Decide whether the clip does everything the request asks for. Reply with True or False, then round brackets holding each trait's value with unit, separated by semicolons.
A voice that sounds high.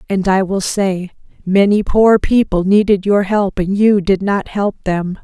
True (195 Hz)